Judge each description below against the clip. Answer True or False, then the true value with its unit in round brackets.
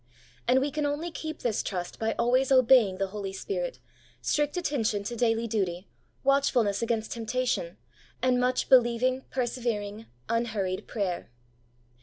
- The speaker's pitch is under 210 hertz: False (235 Hz)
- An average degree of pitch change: True (3.9 semitones)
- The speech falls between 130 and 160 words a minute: True (135 wpm)